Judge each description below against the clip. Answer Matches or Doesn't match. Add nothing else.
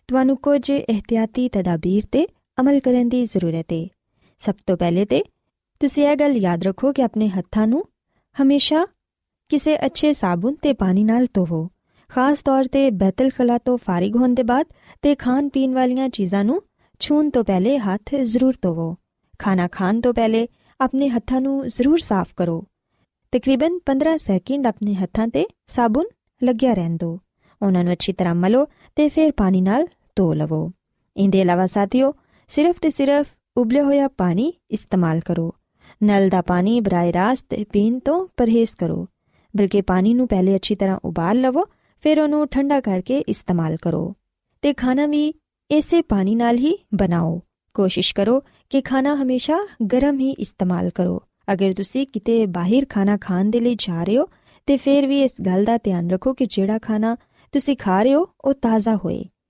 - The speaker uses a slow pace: Doesn't match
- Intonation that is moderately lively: Doesn't match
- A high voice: Matches